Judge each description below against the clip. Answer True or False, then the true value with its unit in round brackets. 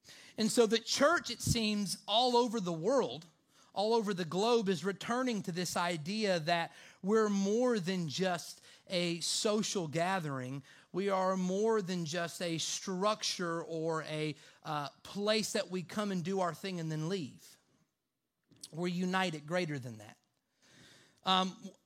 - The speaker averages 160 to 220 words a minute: False (150 wpm)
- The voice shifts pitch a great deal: False (4.0 semitones)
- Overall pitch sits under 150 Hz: False (185 Hz)